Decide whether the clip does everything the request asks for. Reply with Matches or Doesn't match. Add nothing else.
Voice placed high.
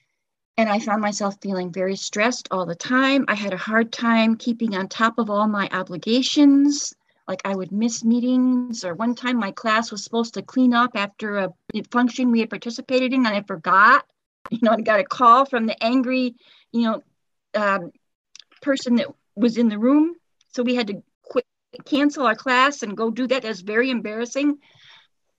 Matches